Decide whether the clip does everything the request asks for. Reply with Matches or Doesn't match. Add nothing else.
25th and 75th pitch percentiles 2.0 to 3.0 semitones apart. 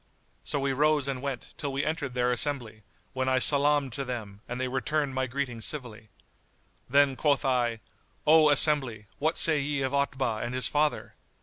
Matches